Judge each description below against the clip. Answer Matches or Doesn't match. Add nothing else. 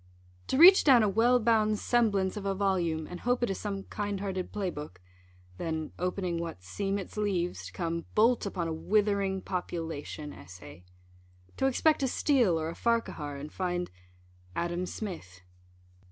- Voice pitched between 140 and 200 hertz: Matches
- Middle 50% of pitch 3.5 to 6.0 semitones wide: Matches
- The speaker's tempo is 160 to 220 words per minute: Matches